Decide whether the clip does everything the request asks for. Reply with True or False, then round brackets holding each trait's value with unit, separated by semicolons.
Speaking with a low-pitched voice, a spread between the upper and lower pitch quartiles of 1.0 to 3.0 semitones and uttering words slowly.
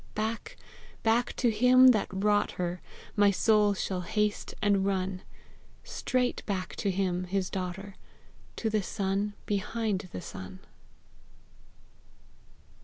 False (200 Hz; 2.6 semitones; 115 wpm)